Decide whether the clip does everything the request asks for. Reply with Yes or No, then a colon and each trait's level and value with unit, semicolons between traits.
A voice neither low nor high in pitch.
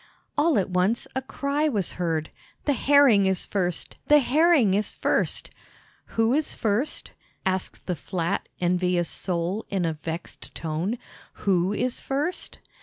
No: high, 200 Hz